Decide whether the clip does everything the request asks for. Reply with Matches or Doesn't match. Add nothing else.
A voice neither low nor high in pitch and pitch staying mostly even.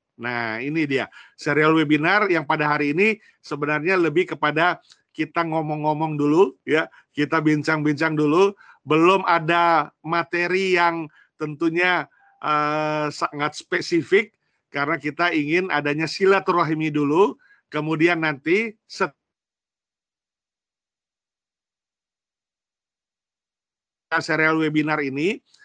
Matches